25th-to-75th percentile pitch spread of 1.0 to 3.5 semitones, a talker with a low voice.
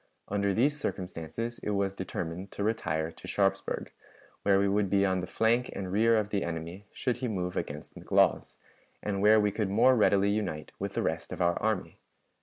Yes: average, 2.8 semitones; low, 100 Hz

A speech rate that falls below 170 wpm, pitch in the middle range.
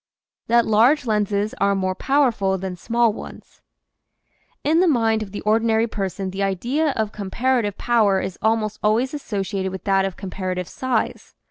No: average, 155 wpm; high, 215 Hz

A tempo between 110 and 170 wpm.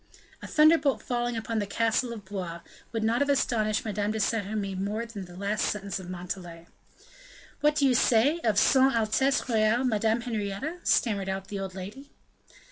No: average, 180 wpm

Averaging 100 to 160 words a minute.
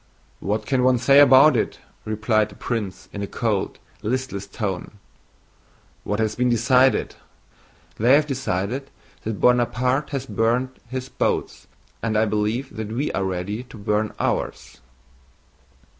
Yes: average, 140 wpm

